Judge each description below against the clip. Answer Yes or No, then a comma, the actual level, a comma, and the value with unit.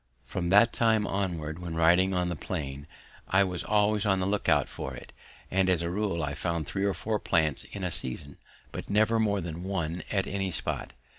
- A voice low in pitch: Yes, very low, 95 Hz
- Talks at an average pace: No, fast, 210 wpm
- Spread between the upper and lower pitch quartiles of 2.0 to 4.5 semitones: Yes, average, 3.4 semitones